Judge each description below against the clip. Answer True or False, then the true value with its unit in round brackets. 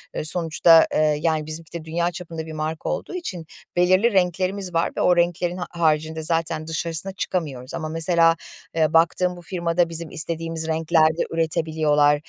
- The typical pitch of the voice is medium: True (165 Hz)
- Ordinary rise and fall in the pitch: False (1.7 semitones)